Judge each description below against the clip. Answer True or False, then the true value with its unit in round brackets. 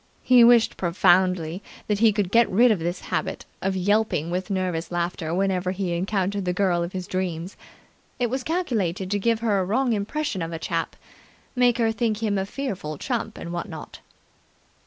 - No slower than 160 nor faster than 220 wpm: True (185 wpm)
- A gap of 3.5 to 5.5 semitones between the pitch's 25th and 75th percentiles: True (4.1 semitones)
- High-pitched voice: True (195 Hz)